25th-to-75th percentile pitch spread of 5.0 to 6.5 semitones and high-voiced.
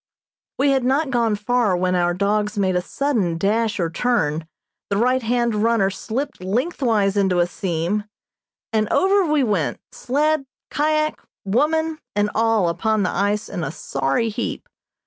Yes: average, 5.3 semitones; high, 215 Hz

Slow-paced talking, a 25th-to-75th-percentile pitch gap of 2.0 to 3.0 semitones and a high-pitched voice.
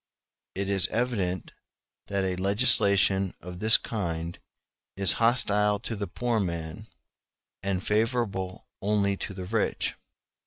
No: slow, 120 wpm; average, 2.7 semitones; low, 100 Hz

